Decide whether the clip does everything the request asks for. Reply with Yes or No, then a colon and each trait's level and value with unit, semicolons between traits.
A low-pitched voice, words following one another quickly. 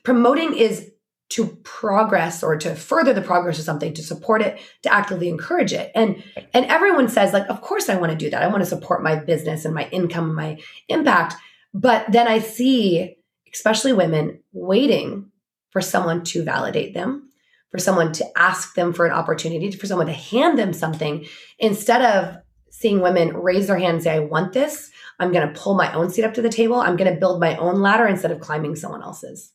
No: medium, 185 Hz; fast, 210 wpm